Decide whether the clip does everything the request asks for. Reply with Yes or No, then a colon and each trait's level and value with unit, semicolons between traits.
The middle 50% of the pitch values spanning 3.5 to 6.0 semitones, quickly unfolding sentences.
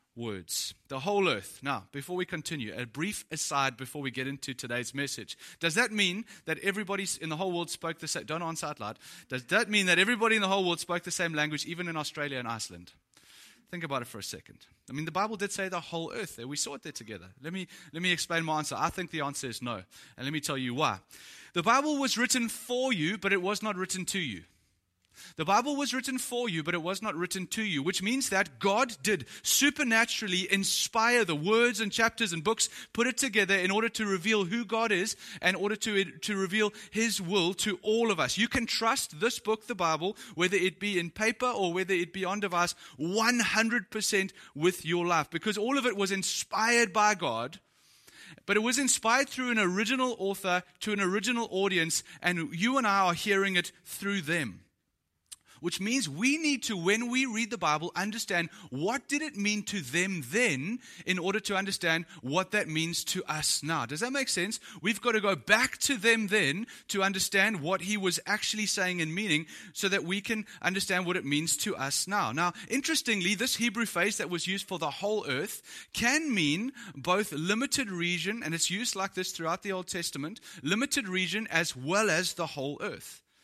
Yes: average, 4.9 semitones; fast, 215 wpm